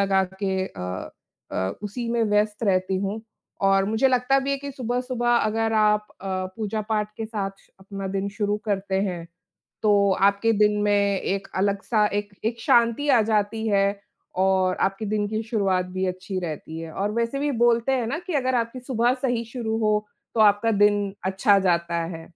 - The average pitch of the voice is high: Yes, high, 210 Hz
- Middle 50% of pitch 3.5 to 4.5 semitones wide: No, average, 2.8 semitones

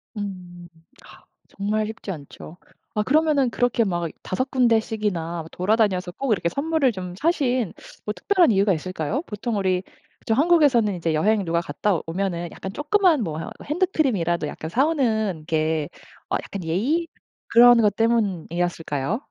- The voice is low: No, high, 210 Hz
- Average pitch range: No, wide, 6.2 semitones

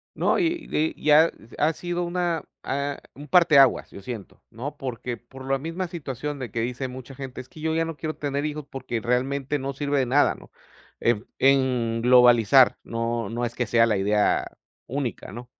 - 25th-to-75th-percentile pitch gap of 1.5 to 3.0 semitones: No, average, 3.7 semitones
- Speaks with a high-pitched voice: No, low, 135 Hz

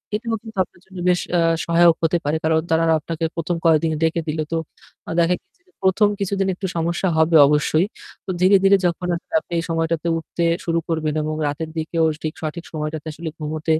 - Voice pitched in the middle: Yes, medium, 165 Hz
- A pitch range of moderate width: No, narrow, 1.9 semitones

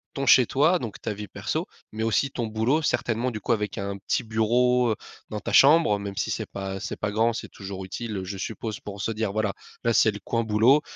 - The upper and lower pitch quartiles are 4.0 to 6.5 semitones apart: No, average, 2.9 semitones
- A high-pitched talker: No, low, 110 Hz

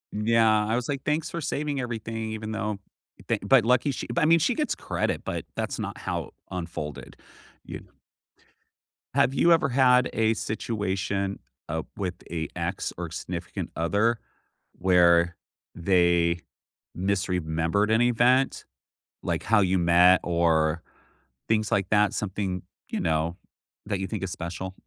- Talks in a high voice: No, low, 100 Hz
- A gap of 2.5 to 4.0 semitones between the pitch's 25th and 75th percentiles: No, average, 4.8 semitones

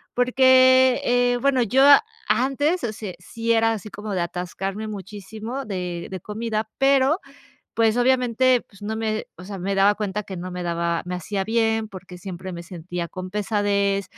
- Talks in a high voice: Yes, high, 210 Hz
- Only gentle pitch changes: No, average, 4.5 semitones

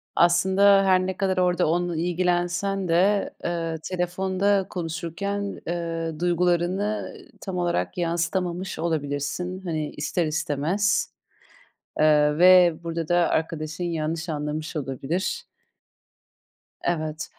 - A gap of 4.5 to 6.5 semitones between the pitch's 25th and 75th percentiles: No, narrow, 2.4 semitones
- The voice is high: No, medium, 175 Hz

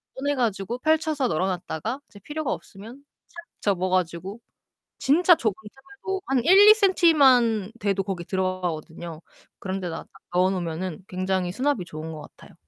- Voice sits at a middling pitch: No, high, 200 Hz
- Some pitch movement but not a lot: No, wide, 7.1 semitones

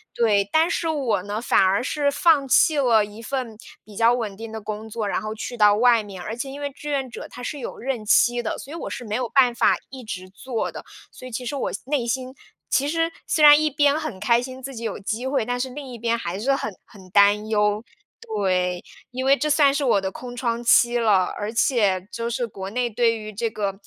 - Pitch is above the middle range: Yes, high, 235 Hz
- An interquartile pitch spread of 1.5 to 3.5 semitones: No, average, 4.1 semitones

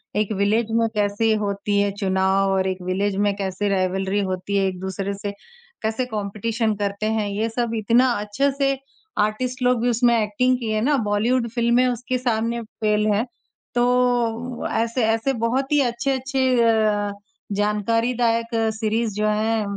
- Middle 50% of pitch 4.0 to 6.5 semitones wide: No, average, 2.8 semitones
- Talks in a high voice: Yes, high, 220 Hz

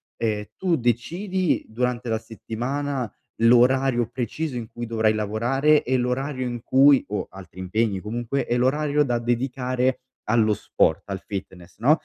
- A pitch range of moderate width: Yes, average, 3.3 semitones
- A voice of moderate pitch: No, low, 120 Hz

